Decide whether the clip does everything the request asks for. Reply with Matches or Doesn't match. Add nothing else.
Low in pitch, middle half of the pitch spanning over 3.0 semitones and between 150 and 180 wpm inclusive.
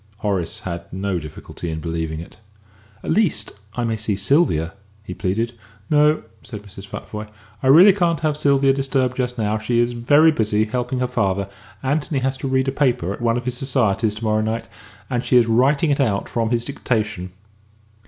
Doesn't match